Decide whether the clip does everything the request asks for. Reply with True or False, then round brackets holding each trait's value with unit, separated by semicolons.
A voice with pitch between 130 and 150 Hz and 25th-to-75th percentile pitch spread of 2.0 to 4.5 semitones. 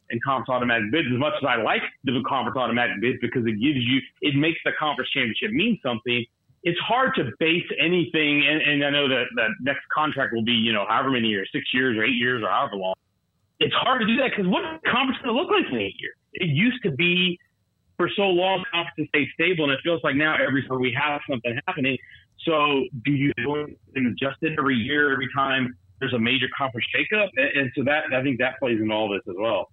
False (135 Hz; 4.9 semitones)